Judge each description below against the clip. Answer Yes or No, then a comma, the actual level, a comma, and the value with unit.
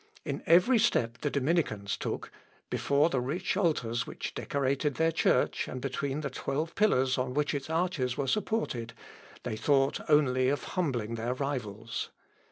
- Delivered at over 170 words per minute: No, average, 155 wpm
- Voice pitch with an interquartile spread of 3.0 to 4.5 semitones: Yes, average, 4.1 semitones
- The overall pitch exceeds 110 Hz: Yes, medium, 140 Hz